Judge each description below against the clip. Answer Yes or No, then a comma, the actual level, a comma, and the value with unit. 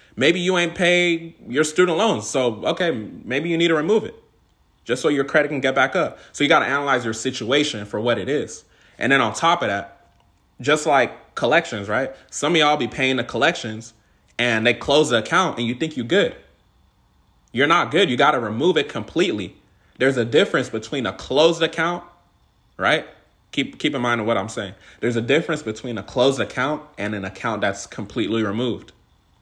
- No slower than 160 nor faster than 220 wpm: Yes, average, 200 wpm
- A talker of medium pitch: No, low, 125 Hz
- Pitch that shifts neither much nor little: No, wide, 6.5 semitones